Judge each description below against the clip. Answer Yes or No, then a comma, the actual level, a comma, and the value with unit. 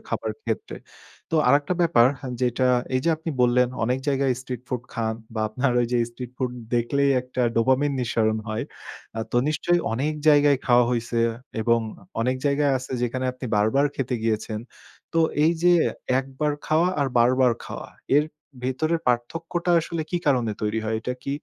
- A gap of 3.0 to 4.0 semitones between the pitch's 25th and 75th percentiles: Yes, average, 3.4 semitones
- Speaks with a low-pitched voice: Yes, low, 130 Hz